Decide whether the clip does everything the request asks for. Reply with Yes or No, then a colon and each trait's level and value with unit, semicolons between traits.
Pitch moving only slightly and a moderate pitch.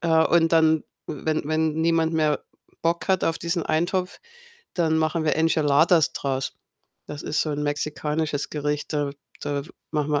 Yes: narrow, 1.8 semitones; medium, 155 Hz